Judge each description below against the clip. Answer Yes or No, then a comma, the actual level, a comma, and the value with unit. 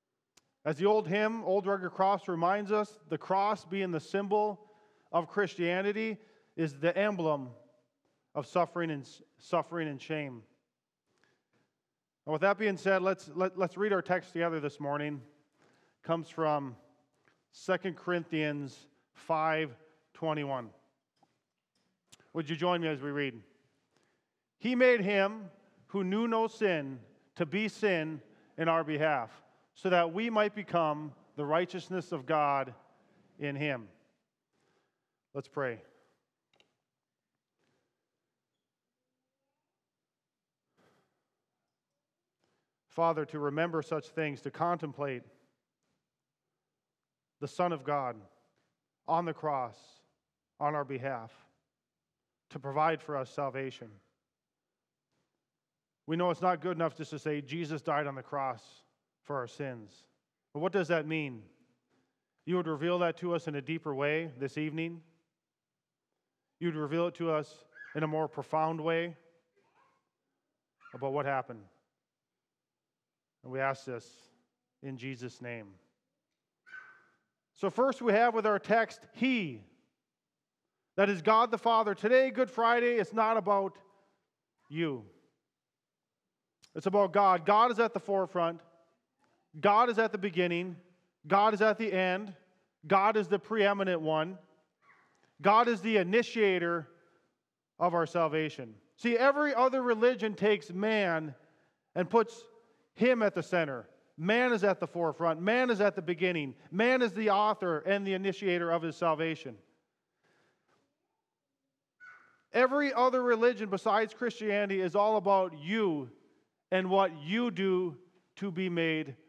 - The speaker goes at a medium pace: No, slow, 125 wpm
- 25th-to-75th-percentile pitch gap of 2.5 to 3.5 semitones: No, average, 5.0 semitones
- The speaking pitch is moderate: Yes, medium, 170 Hz